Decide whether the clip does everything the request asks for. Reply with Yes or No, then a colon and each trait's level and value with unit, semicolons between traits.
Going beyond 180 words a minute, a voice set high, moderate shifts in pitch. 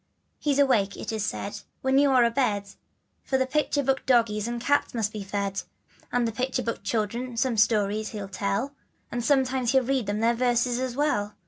Yes: average, 195 wpm; high, 235 Hz; average, 3.8 semitones